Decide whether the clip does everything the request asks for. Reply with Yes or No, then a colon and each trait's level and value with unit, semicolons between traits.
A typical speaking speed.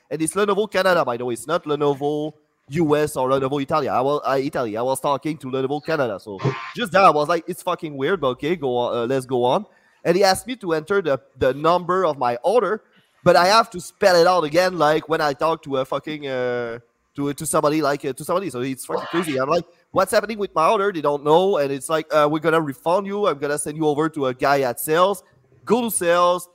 No: fast, 255 wpm